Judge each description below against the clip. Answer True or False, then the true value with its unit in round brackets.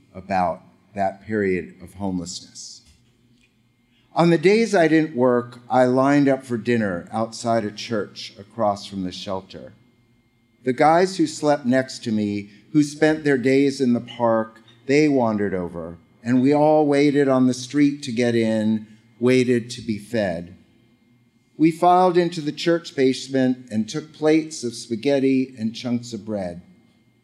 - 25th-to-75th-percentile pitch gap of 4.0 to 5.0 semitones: True (4.3 semitones)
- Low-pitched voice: True (120 Hz)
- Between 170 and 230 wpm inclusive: False (150 wpm)